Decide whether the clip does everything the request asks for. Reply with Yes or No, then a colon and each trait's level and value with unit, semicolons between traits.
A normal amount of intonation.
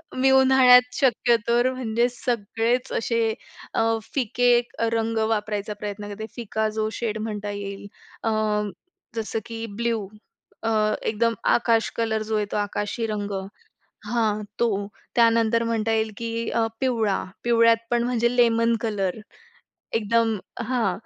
No: narrow, 1.7 semitones